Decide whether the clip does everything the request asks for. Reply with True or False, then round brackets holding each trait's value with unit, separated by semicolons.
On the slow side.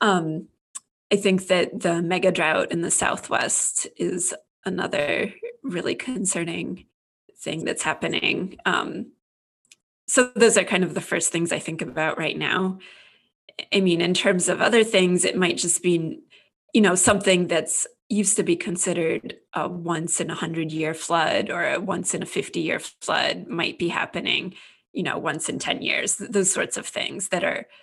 False (170 wpm)